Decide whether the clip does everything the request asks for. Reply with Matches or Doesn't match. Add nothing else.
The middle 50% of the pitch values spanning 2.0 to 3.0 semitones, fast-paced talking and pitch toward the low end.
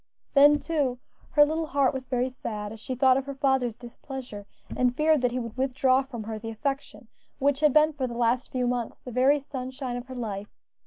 Doesn't match